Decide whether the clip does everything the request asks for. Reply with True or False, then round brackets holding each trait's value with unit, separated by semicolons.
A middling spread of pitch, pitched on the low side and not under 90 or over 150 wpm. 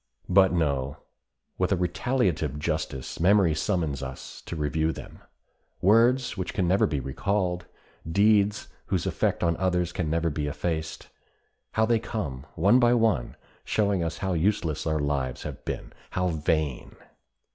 True (4.6 semitones; 85 Hz; 145 wpm)